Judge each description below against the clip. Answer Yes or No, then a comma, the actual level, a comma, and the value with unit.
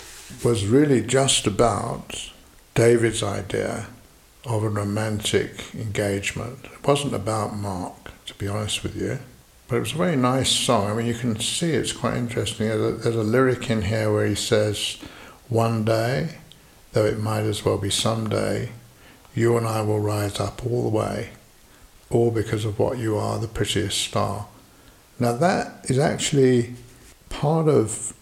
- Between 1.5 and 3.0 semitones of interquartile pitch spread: Yes, narrow, 2.4 semitones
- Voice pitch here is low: Yes, low, 110 Hz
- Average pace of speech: Yes, average, 165 wpm